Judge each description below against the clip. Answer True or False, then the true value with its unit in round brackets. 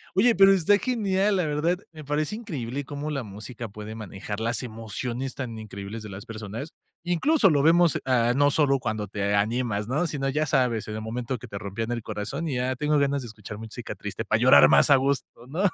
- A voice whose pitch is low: True (130 Hz)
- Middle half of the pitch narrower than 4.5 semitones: False (5.6 semitones)